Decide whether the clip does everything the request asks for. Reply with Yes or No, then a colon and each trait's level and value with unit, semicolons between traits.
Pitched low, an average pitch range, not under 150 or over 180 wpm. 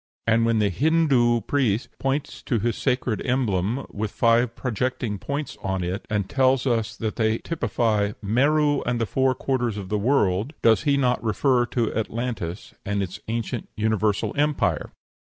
Yes: low, 115 Hz; average, 3.8 semitones; average, 160 wpm